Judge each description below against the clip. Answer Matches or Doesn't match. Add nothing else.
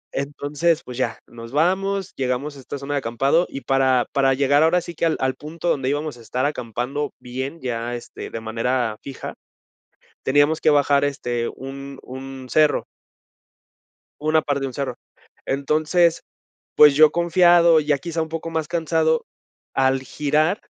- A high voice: Doesn't match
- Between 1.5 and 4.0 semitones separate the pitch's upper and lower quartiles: Matches